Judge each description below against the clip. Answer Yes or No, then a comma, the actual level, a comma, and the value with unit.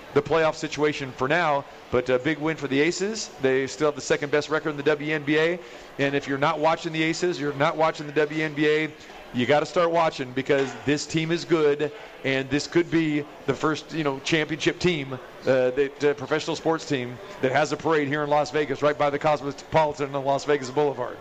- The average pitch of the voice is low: No, medium, 150 Hz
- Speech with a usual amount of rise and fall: No, narrow, 2.2 semitones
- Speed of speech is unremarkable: No, fast, 215 wpm